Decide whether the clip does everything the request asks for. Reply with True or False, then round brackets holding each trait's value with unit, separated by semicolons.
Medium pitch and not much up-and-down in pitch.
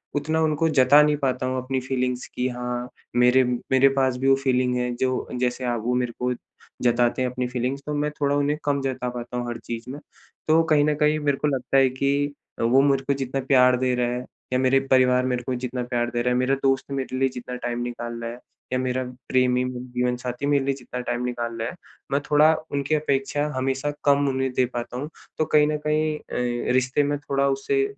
False (130 Hz; 2.1 semitones)